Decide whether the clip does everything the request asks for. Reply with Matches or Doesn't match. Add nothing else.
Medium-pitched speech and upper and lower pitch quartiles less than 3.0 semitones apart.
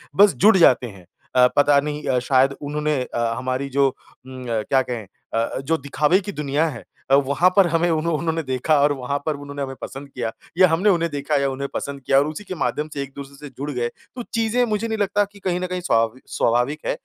Doesn't match